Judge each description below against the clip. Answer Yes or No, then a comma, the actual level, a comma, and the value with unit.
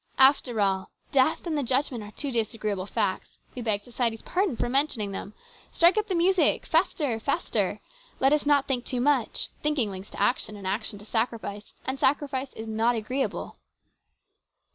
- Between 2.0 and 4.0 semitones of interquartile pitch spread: No, average, 4.8 semitones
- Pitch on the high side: Yes, high, 245 Hz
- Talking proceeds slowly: No, average, 175 wpm